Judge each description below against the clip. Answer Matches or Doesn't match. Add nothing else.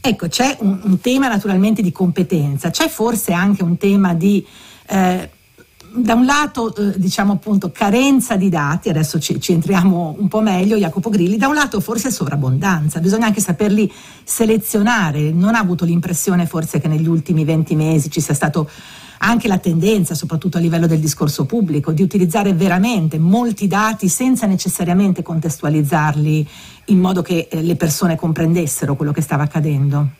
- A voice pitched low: Doesn't match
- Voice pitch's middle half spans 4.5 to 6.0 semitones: Doesn't match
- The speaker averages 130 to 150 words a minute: Doesn't match